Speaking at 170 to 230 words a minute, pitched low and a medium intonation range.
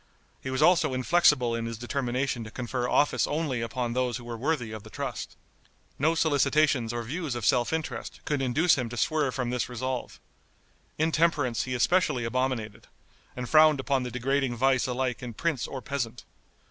Yes: average, 175 wpm; low, 130 Hz; average, 3.3 semitones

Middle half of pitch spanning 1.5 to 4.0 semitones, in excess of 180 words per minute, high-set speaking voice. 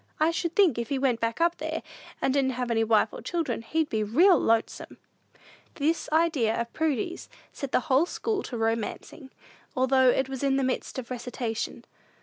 No: average, 5.3 semitones; average, 190 wpm; very high, 260 Hz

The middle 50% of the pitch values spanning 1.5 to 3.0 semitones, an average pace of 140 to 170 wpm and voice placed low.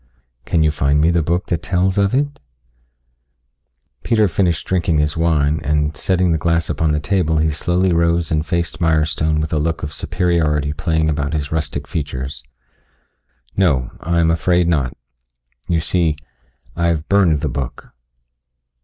Yes: narrow, 2.4 semitones; average, 160 wpm; very low, 80 Hz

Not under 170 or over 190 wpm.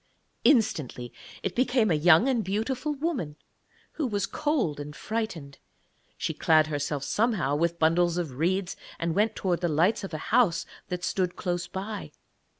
No: average, 155 wpm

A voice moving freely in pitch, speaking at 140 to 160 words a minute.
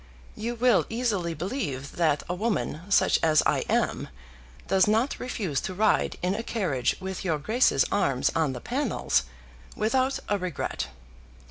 Yes: wide, 6.5 semitones; average, 150 wpm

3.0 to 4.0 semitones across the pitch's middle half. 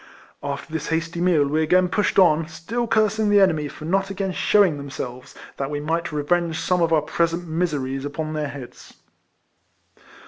Yes: average, 3.5 semitones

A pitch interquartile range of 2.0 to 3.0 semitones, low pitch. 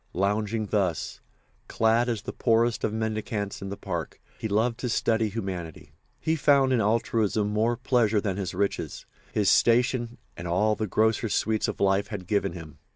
Yes: narrow, 2.5 semitones; low, 110 Hz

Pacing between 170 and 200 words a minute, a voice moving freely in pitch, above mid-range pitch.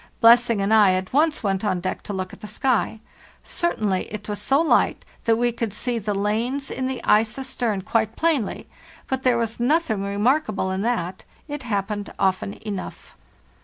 No: average, 180 wpm; average, 3.9 semitones; high, 220 Hz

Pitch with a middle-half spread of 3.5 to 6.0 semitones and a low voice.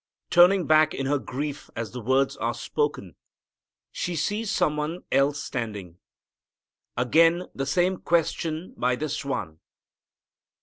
No: average, 4.8 semitones; medium, 145 Hz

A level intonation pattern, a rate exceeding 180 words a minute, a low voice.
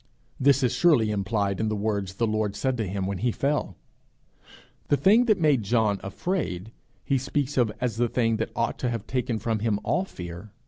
No: average, 4.5 semitones; average, 200 wpm; low, 115 Hz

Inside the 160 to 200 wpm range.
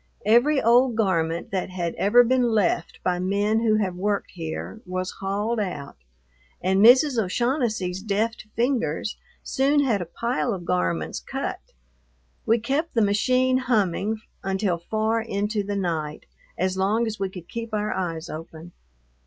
No: average, 150 wpm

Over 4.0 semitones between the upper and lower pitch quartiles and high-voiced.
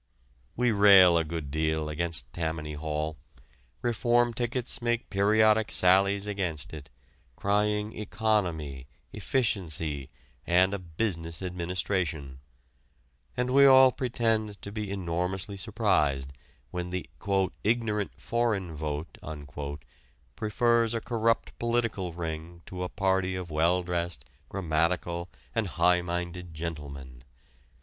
No: average, 5.1 semitones; very low, 90 Hz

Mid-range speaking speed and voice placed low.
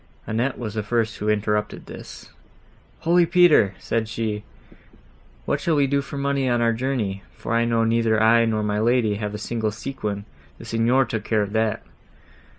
Yes: average, 180 wpm; low, 115 Hz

